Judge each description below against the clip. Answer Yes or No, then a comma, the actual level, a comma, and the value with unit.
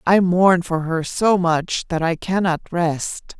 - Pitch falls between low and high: Yes, medium, 175 Hz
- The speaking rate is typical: Yes, average, 175 wpm